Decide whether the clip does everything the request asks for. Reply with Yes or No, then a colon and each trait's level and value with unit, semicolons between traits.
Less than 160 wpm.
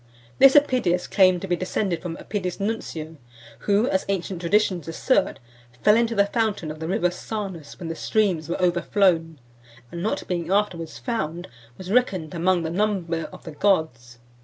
No: average, 170 wpm